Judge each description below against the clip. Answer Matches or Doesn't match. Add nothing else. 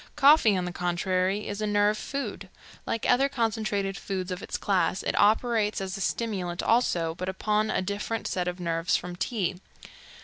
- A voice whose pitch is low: Doesn't match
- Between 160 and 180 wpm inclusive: Matches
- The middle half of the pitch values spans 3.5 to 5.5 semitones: Doesn't match